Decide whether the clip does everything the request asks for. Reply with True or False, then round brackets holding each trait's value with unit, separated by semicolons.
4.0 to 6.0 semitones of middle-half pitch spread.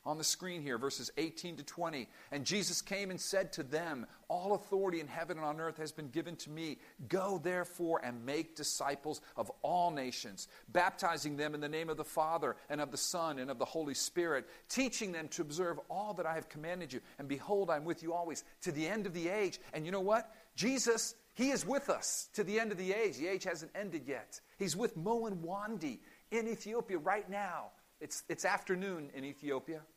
True (4.5 semitones)